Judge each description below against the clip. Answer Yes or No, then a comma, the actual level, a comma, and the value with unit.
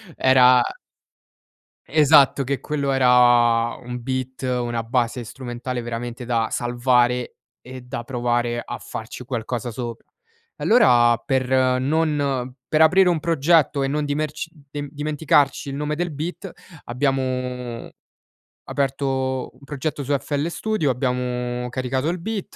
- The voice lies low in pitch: Yes, low, 130 Hz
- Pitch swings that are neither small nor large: Yes, average, 3.0 semitones